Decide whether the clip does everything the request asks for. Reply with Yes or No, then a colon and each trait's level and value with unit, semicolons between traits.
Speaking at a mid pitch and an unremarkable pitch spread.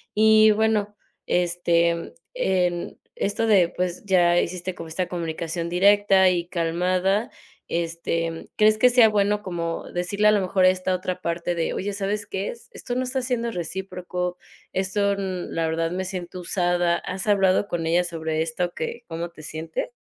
Yes: medium, 180 Hz; average, 3.0 semitones